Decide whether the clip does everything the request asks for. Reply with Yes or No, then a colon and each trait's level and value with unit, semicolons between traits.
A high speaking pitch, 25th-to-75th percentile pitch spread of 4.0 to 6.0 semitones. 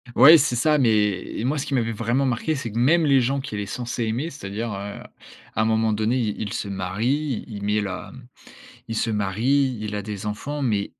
No: low, 115 Hz; average, 4.4 semitones